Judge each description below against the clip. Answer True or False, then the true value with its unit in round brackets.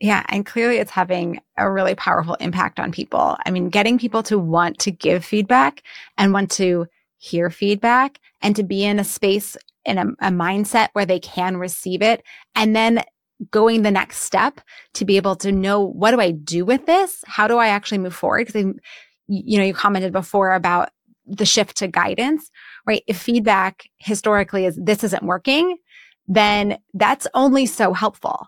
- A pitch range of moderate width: True (3.2 semitones)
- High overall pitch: True (205 Hz)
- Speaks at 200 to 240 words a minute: False (185 wpm)